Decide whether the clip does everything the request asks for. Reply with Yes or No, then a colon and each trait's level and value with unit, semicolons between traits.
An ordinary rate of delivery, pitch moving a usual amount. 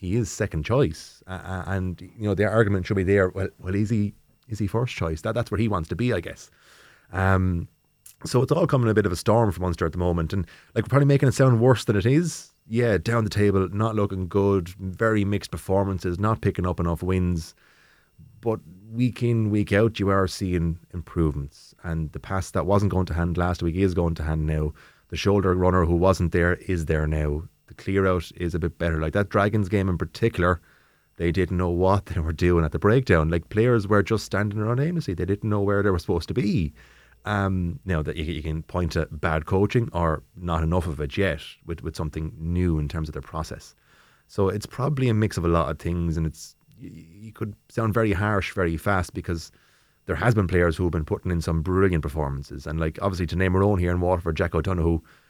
No: fast, 230 wpm; average, 3.7 semitones